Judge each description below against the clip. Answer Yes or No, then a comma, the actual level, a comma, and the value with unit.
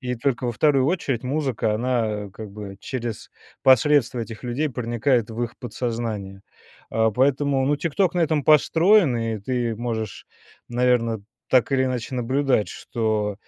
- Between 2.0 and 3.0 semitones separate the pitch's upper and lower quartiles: No, average, 3.4 semitones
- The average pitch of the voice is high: No, low, 125 Hz